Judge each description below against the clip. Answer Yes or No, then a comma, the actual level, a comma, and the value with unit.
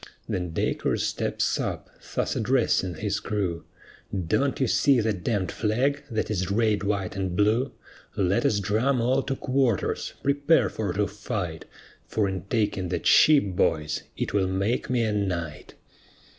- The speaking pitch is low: Yes, low, 105 Hz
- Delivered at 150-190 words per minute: Yes, average, 155 wpm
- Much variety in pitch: No, average, 4.3 semitones